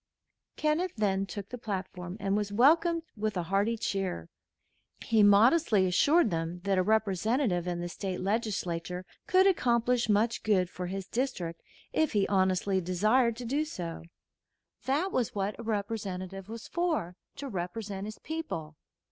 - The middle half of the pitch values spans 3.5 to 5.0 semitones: Yes, average, 4.5 semitones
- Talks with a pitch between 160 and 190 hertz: No, high, 205 Hz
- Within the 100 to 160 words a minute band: Yes, average, 150 wpm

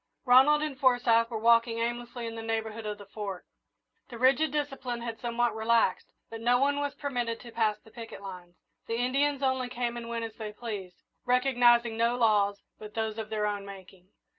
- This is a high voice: Yes, high, 230 Hz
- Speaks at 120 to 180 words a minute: No, average, 190 wpm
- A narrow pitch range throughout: Yes, narrow, 2.2 semitones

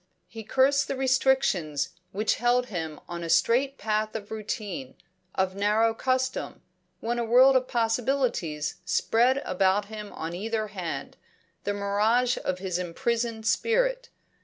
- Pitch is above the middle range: Yes, high, 220 Hz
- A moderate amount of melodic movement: Yes, average, 4.7 semitones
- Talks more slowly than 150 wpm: Yes, slow, 135 wpm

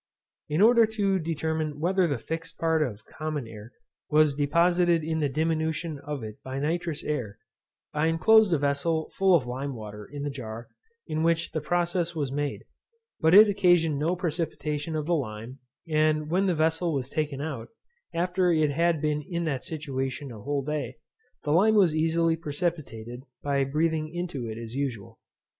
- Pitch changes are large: No, average, 3.2 semitones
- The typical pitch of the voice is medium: Yes, medium, 155 Hz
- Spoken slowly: No, average, 175 wpm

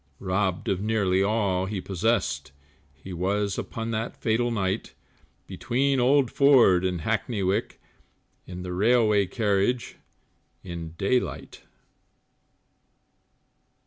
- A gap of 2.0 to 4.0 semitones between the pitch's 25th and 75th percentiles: Yes, average, 3.7 semitones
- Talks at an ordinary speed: No, slow, 110 wpm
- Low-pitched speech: Yes, low, 100 Hz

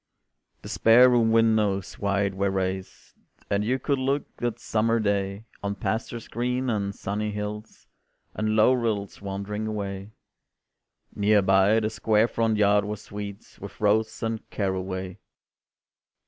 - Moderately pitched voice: No, low, 105 Hz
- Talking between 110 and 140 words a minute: Yes, slow, 135 wpm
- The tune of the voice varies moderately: No, narrow, 2.2 semitones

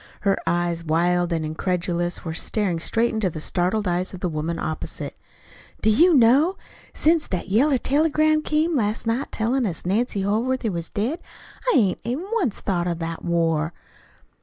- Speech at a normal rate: Yes, average, 165 wpm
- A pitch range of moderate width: No, wide, 6.8 semitones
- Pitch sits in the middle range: No, high, 195 Hz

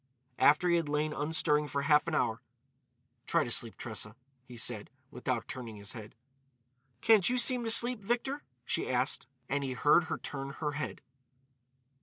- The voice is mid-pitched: Yes, medium, 150 Hz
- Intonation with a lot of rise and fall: Yes, wide, 5.7 semitones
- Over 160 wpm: Yes, average, 170 wpm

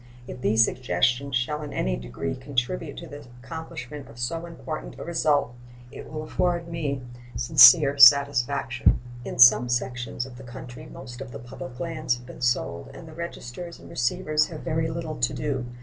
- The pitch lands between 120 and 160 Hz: Yes, low, 135 Hz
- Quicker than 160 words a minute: Yes, average, 175 wpm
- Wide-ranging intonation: No, average, 4.2 semitones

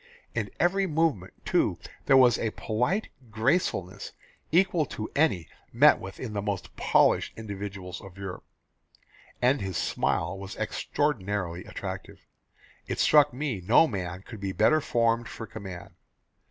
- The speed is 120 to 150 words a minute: Yes, average, 140 wpm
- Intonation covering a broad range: Yes, wide, 6.5 semitones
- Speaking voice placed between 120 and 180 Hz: No, low, 110 Hz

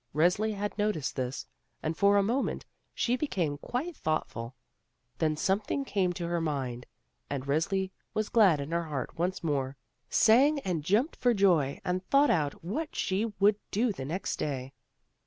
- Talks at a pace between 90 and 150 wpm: No, average, 165 wpm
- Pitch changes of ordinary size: No, wide, 6.0 semitones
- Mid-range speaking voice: Yes, medium, 180 Hz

